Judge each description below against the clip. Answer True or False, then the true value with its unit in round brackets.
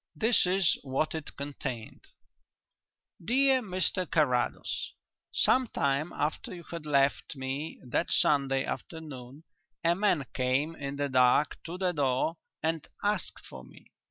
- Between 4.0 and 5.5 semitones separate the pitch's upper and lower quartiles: True (4.6 semitones)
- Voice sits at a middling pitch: True (150 Hz)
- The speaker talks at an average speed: False (130 wpm)